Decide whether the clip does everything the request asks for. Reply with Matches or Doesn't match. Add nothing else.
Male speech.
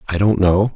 Matches